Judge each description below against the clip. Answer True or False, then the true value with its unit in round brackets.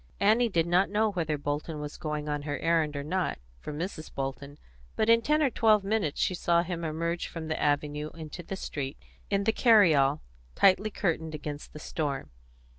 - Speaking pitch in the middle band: True (165 Hz)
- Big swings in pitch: False (4.8 semitones)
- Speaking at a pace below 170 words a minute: False (190 wpm)